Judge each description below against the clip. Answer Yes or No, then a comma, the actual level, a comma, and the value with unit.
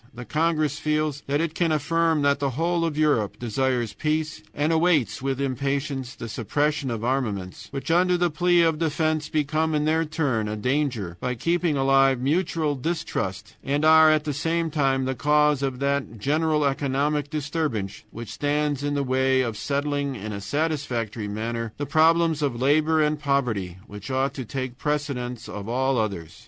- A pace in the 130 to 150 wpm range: No, average, 175 wpm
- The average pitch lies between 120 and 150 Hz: Yes, medium, 140 Hz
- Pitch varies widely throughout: No, average, 3.6 semitones